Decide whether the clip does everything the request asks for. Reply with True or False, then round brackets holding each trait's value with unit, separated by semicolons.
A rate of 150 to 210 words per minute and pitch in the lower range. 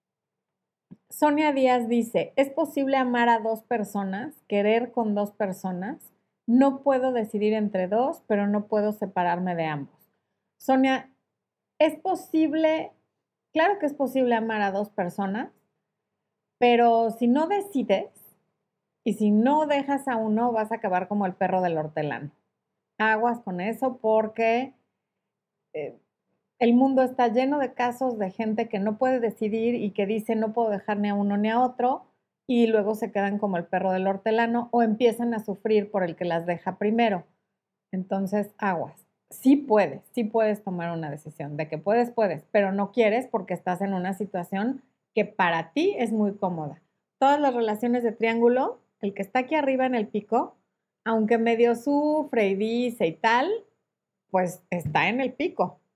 False (165 wpm; 220 Hz)